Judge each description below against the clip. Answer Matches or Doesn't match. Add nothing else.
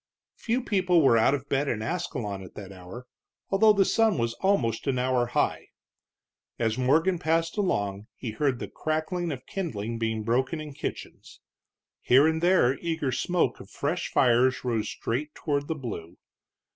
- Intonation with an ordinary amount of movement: Doesn't match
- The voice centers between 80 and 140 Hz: Matches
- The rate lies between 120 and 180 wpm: Matches